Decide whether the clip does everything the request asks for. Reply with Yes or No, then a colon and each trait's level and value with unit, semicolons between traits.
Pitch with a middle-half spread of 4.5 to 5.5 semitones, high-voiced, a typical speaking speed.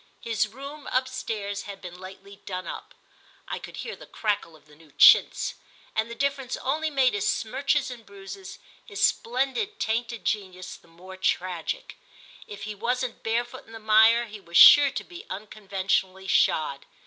Yes: average, 5.1 semitones; high, 220 Hz; average, 165 wpm